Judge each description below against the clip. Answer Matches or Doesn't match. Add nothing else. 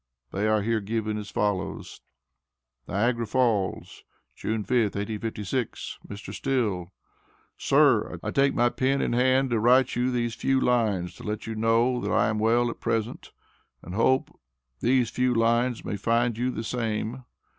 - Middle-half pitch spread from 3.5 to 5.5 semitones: Doesn't match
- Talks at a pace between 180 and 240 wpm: Doesn't match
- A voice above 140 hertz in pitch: Doesn't match